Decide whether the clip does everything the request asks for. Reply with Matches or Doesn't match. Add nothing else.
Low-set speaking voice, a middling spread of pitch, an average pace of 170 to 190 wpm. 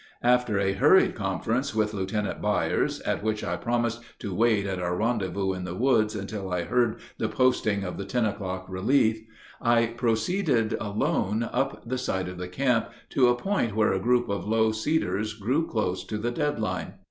Matches